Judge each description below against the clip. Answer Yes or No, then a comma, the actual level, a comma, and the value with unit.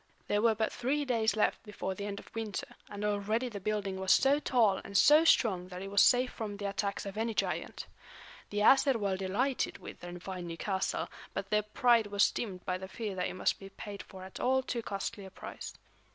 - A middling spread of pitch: Yes, average, 3.0 semitones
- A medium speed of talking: No, fast, 225 wpm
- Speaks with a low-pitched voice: No, high, 205 Hz